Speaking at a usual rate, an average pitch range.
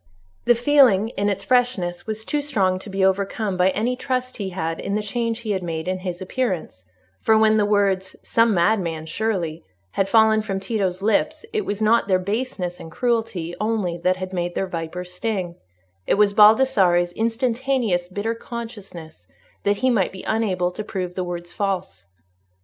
Yes: average, 175 wpm; average, 3.9 semitones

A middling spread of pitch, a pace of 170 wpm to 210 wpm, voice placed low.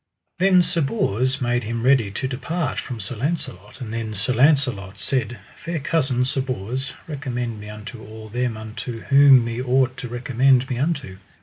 Yes: average, 3.2 semitones; average, 175 wpm; low, 125 Hz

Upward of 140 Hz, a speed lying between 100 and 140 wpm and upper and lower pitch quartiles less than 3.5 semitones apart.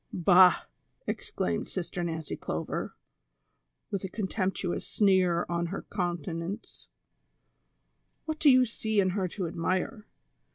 Yes: medium, 185 Hz; slow, 135 wpm; average, 2.9 semitones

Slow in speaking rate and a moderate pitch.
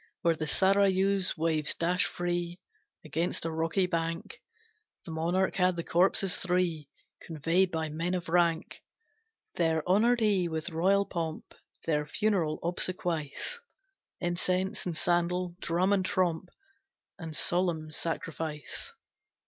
Yes: slow, 120 wpm; medium, 175 Hz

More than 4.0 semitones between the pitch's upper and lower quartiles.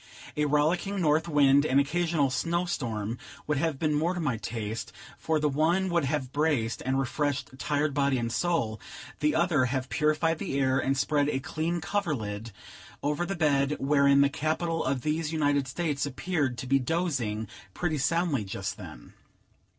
No: average, 3.4 semitones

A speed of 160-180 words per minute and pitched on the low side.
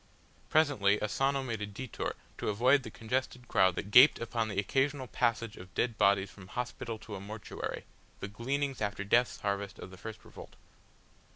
Yes: average, 175 wpm; low, 110 Hz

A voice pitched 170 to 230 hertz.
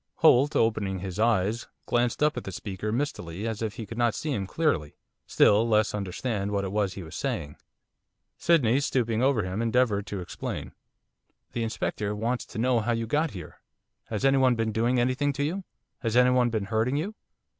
No: low, 115 Hz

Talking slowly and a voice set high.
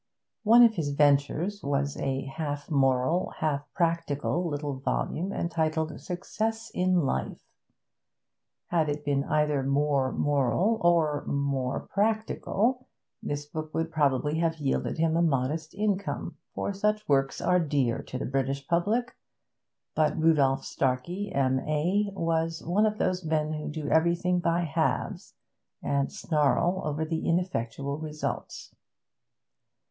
No: slow, 130 wpm; medium, 155 Hz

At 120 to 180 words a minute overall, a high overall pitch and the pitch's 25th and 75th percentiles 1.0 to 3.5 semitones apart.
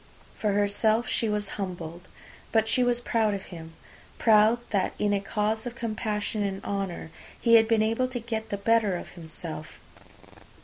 Yes: average, 170 wpm; high, 210 Hz; narrow, 2.4 semitones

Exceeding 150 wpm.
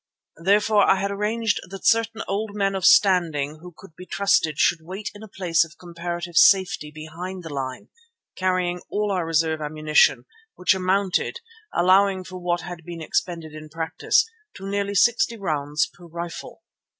Yes: average, 160 wpm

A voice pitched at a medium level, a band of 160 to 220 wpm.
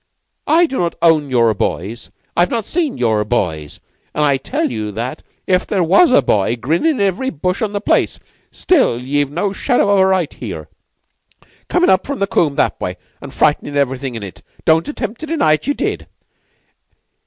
Yes: medium, 170 Hz; average, 190 wpm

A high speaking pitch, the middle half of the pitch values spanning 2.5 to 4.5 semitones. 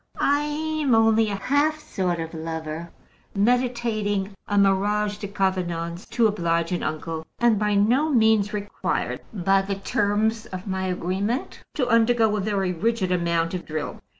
Yes: high, 205 Hz; average, 3.8 semitones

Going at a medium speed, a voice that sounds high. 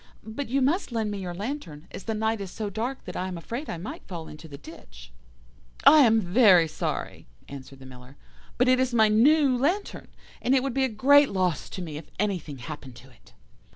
No: fast, 220 wpm; high, 210 Hz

